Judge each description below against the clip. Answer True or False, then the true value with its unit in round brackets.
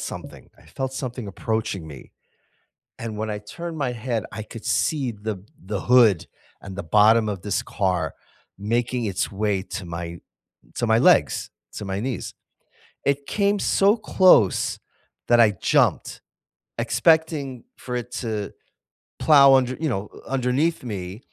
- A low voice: True (115 Hz)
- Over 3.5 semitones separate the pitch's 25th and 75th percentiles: True (4.7 semitones)